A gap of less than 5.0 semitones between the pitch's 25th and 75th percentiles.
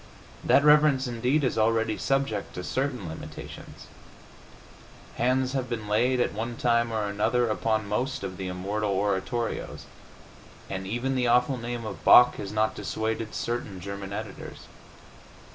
Yes: average, 3.2 semitones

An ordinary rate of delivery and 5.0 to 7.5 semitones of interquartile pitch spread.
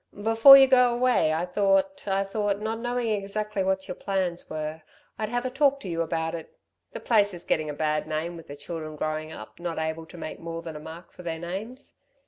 No: fast, 225 wpm; average, 5.3 semitones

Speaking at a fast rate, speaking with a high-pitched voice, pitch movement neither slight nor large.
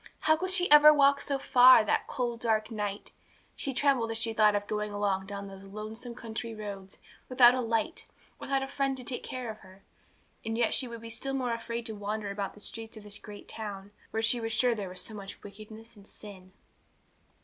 Yes: fast, 215 wpm; high, 225 Hz; average, 3.3 semitones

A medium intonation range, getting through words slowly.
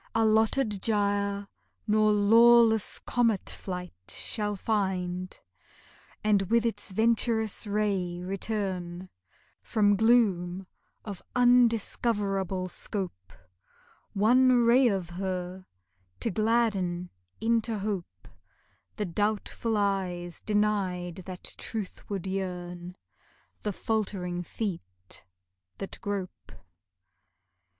Yes: average, 3.4 semitones; slow, 85 wpm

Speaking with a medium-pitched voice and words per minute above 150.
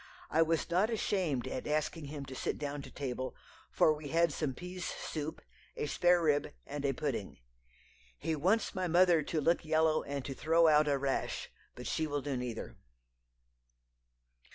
Yes: medium, 155 Hz; average, 170 wpm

